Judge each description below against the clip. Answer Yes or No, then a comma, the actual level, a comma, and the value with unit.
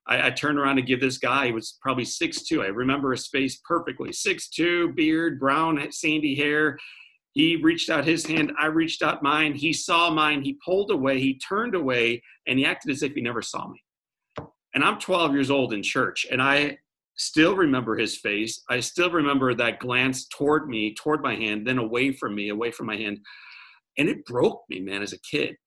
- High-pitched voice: No, medium, 140 Hz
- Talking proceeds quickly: Yes, fast, 210 wpm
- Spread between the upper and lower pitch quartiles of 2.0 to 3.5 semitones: No, average, 4.3 semitones